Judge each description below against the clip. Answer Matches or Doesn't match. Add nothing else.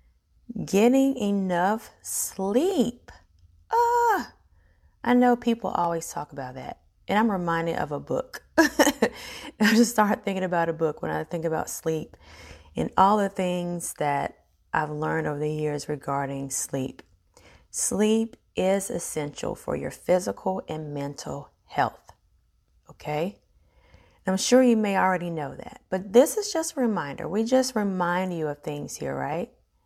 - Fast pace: Doesn't match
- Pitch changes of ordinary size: Doesn't match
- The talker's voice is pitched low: Doesn't match